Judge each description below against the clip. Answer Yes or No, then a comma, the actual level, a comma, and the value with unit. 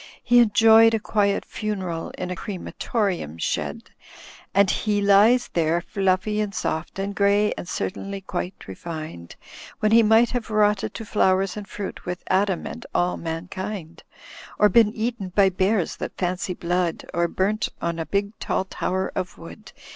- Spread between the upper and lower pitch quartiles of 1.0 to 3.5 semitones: Yes, average, 2.9 semitones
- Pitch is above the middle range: Yes, high, 195 Hz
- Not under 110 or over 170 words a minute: Yes, average, 160 wpm